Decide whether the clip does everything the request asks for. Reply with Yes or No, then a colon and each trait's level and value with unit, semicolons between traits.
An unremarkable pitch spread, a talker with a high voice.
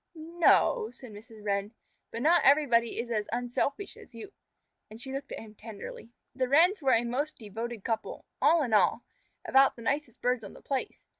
Yes: average, 4.2 semitones; high, 245 Hz